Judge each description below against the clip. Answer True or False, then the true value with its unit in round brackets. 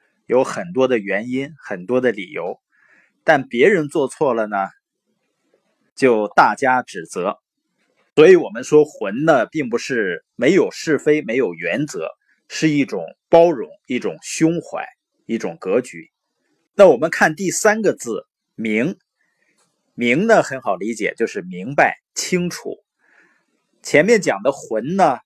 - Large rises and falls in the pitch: True (6.6 semitones)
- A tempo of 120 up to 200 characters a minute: True (195 characters per minute)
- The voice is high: False (150 Hz)